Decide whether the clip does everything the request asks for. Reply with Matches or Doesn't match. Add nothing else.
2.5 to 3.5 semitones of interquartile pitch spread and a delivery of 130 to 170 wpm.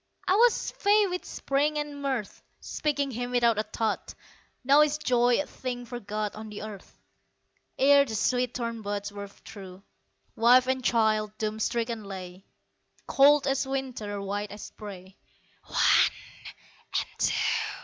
Doesn't match